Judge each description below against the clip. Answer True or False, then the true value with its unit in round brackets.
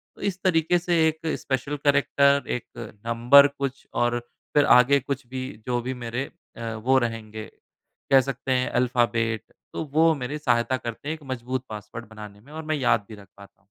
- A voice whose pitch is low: True (130 Hz)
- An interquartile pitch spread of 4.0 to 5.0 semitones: False (3.3 semitones)